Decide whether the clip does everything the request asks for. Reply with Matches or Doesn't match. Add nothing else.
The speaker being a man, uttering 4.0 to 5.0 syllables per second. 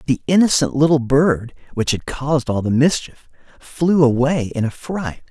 Matches